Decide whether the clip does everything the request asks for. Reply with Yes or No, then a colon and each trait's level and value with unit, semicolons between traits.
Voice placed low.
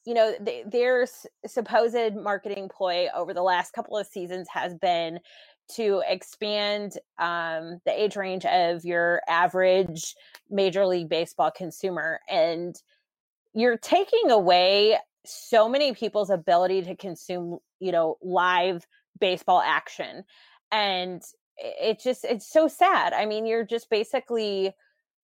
No: high, 195 Hz